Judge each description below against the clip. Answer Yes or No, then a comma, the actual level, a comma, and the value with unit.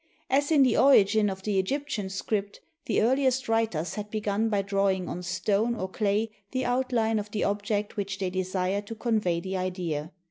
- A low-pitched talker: No, high, 205 Hz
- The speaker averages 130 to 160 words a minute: No, average, 180 wpm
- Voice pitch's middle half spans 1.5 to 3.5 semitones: Yes, average, 3.0 semitones